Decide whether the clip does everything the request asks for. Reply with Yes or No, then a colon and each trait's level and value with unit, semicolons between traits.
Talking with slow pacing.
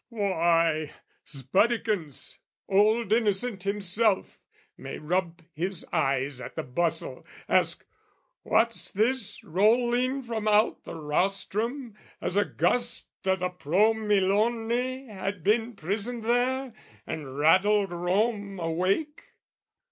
Yes: slow, 105 wpm